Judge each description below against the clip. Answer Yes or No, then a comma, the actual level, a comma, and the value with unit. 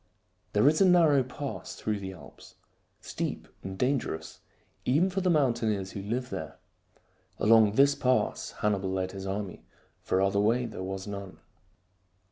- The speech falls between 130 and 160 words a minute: Yes, average, 150 wpm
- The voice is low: Yes, low, 110 Hz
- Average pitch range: No, wide, 5.7 semitones